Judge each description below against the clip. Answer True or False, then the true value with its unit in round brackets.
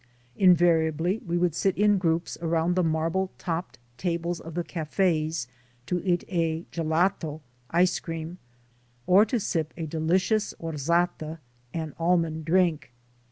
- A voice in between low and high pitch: True (170 Hz)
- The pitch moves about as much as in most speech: False (2.0 semitones)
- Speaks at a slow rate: True (130 wpm)